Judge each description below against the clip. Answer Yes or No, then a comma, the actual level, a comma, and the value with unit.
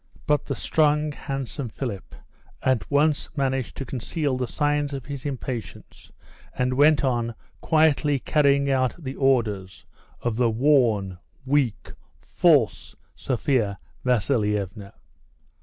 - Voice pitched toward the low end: Yes, low, 130 Hz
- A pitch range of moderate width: Yes, average, 3.8 semitones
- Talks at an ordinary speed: No, slow, 115 wpm